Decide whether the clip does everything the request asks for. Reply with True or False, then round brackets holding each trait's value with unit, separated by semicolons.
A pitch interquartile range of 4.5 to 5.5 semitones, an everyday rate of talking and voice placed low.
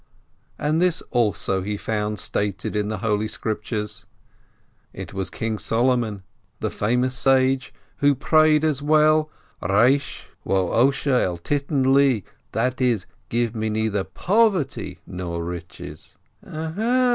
False (5.0 semitones; 120 wpm; 120 Hz)